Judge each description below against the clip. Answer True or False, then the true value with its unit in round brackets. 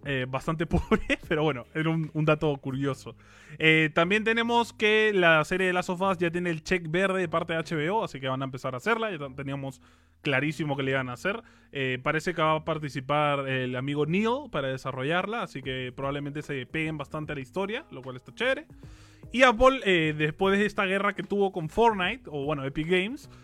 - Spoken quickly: True (210 wpm)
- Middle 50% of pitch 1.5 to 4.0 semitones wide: False (5.4 semitones)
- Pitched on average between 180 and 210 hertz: False (155 Hz)